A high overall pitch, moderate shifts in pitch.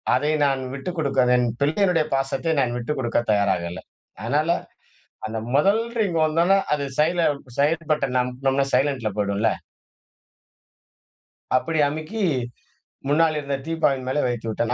No: medium, 140 Hz; average, 4.1 semitones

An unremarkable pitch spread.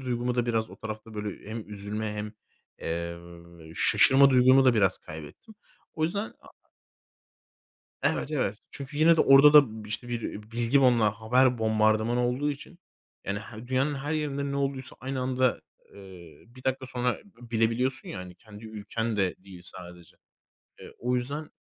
Yes: average, 4.0 semitones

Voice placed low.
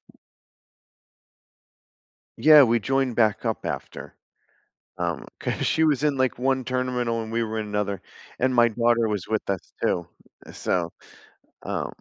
Yes: low, 115 Hz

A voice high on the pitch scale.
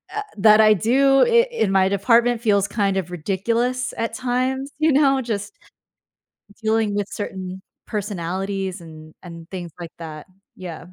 Yes: high, 205 Hz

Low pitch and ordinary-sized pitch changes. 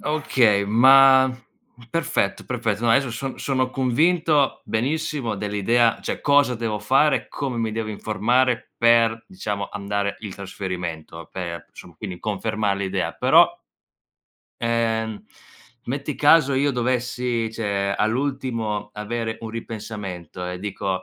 Yes: low, 115 Hz; average, 4.3 semitones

